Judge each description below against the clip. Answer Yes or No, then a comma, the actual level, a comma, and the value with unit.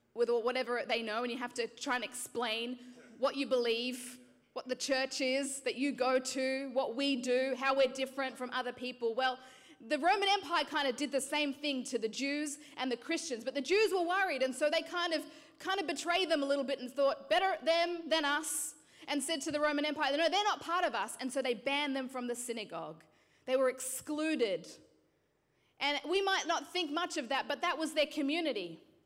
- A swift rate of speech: Yes, fast, 225 wpm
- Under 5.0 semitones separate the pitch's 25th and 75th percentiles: Yes, average, 3.7 semitones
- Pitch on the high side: Yes, very high, 275 Hz